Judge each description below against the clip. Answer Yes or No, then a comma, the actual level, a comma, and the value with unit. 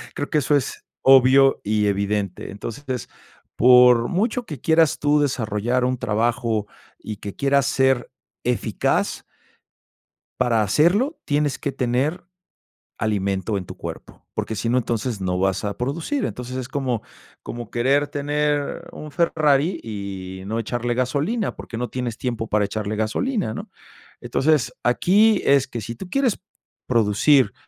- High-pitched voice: No, low, 125 Hz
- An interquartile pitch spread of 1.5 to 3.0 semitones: No, average, 5.0 semitones